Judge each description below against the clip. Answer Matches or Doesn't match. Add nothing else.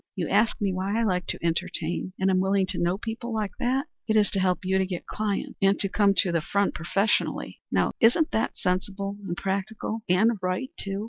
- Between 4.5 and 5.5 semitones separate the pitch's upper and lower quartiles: Doesn't match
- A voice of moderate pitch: Doesn't match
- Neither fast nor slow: Doesn't match